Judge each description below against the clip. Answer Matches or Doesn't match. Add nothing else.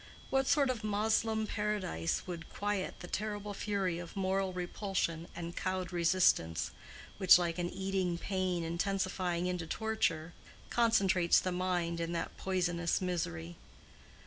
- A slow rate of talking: Matches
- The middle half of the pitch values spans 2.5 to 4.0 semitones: Matches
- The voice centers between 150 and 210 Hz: Matches